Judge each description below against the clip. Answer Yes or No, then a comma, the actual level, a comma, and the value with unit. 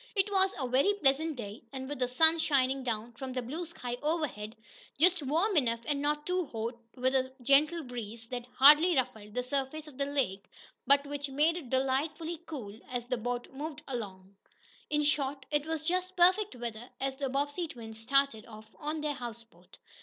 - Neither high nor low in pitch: No, very high, 275 Hz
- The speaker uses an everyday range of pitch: Yes, average, 4.0 semitones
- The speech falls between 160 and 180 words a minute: No, average, 190 wpm